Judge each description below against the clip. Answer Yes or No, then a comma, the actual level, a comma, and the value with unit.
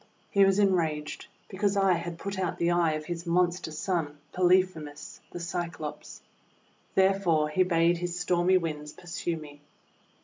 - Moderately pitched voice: Yes, medium, 175 Hz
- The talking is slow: No, average, 145 wpm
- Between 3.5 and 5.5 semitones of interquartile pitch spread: No, narrow, 2.6 semitones